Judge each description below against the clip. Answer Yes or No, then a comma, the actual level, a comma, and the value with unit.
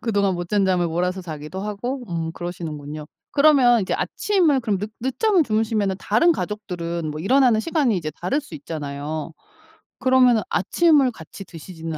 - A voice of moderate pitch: No, high, 195 Hz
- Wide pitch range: Yes, wide, 7.2 semitones